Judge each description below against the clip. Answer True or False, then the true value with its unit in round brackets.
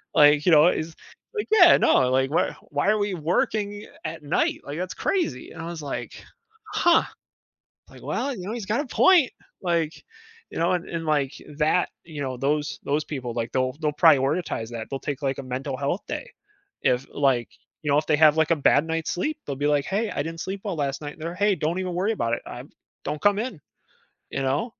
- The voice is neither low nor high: True (155 Hz)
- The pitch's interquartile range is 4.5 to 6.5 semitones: True (4.8 semitones)